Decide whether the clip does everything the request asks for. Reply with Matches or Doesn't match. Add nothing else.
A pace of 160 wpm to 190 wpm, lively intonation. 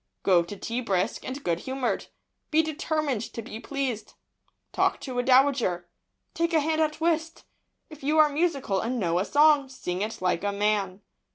Matches